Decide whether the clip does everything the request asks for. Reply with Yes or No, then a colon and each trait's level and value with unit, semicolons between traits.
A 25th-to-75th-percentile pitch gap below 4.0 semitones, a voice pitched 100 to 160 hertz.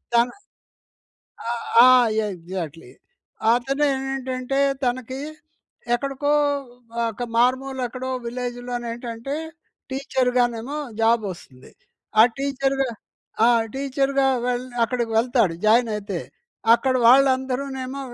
No: narrow, 2.4 semitones; very high, 250 Hz